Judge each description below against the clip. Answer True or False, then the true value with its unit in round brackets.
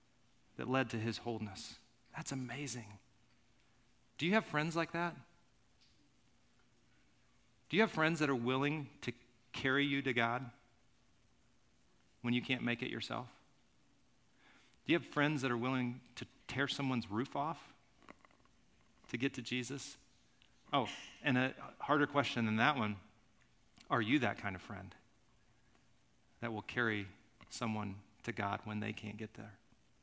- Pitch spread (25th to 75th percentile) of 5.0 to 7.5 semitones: False (4.1 semitones)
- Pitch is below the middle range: True (120 Hz)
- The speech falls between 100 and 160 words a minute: True (145 wpm)